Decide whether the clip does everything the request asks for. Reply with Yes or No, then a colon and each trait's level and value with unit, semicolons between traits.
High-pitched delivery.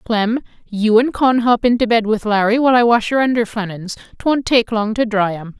Yes: high, 225 Hz